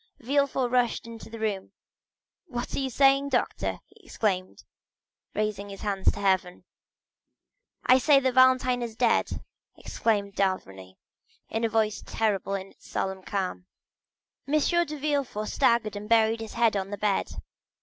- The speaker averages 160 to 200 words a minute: No, average, 150 wpm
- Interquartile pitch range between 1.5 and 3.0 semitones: No, average, 4.3 semitones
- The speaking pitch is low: No, high, 220 Hz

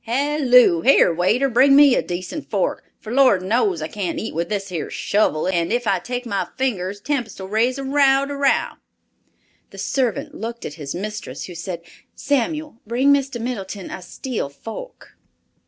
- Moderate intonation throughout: No, wide, 6.4 semitones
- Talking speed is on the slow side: No, average, 170 wpm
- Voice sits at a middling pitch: No, high, 230 Hz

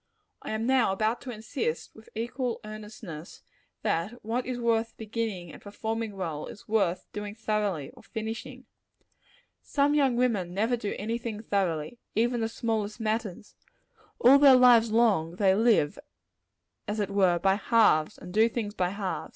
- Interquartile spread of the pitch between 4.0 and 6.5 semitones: No, average, 3.0 semitones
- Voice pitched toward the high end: Yes, high, 220 Hz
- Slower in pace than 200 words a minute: Yes, average, 160 wpm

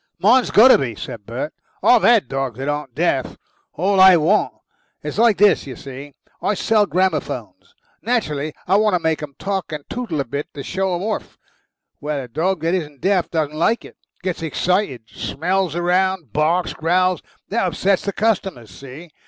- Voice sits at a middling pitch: Yes, medium, 170 Hz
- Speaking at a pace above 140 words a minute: Yes, average, 180 wpm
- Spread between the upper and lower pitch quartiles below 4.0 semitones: No, average, 5.1 semitones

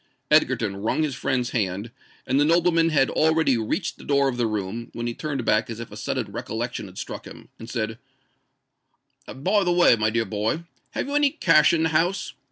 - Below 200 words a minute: No, fast, 205 wpm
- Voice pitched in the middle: No, low, 130 Hz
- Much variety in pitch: Yes, wide, 6.3 semitones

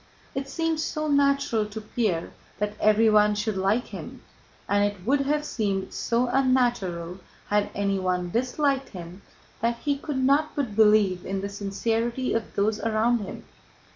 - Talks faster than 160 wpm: No, average, 150 wpm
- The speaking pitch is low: No, high, 220 Hz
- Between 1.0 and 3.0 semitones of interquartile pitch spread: No, average, 4.6 semitones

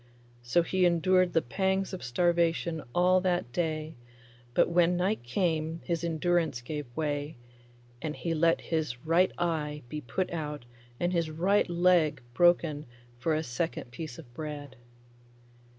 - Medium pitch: Yes, medium, 165 Hz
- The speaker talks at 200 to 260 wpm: No, average, 145 wpm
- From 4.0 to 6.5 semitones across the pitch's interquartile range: No, average, 2.7 semitones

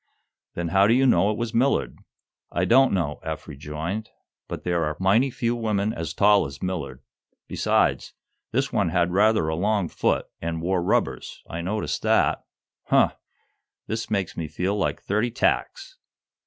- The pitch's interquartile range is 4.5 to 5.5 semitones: Yes, average, 4.8 semitones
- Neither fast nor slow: Yes, average, 165 wpm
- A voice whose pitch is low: Yes, very low, 95 Hz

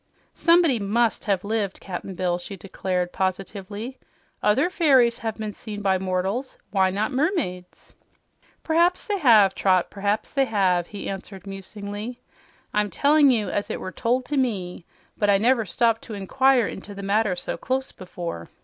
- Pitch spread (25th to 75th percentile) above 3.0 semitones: Yes, average, 4.6 semitones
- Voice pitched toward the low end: No, high, 205 Hz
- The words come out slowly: No, average, 160 wpm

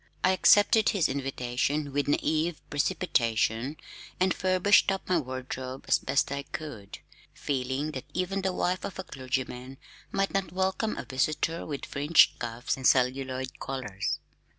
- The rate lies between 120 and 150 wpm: Yes, average, 145 wpm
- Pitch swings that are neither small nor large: No, wide, 5.9 semitones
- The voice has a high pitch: No, medium, 140 Hz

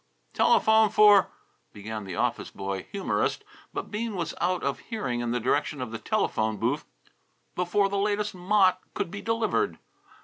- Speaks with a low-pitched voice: No, medium, 185 Hz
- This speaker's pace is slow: No, average, 165 wpm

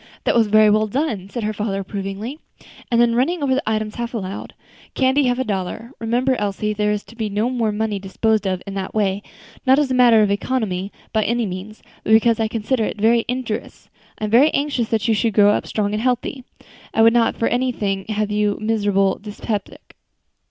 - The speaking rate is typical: No, fast, 215 wpm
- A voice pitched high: Yes, high, 220 Hz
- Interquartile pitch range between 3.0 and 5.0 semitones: No, narrow, 2.6 semitones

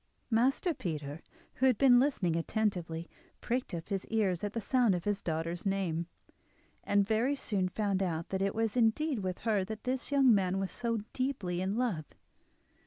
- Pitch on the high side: Yes, high, 205 Hz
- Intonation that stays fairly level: No, average, 4.8 semitones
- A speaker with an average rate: Yes, average, 175 wpm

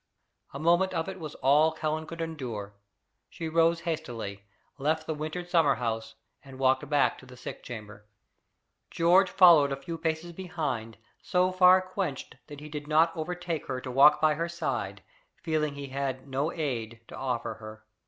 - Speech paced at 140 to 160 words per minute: No, average, 175 wpm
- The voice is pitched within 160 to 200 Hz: No, medium, 150 Hz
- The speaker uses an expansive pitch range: No, average, 4.2 semitones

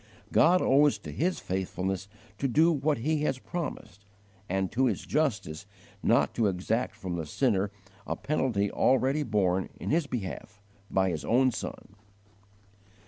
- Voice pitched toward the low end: Yes, low, 115 Hz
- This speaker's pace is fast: No, average, 145 wpm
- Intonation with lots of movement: Yes, wide, 6.8 semitones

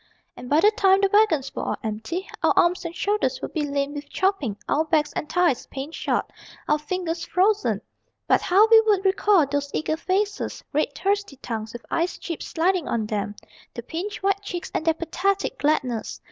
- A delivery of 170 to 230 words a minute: Yes, average, 190 wpm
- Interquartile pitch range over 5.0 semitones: Yes, wide, 5.4 semitones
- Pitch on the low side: No, very high, 335 Hz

